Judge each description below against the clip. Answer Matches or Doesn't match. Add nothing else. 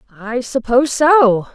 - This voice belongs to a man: Doesn't match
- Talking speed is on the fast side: Doesn't match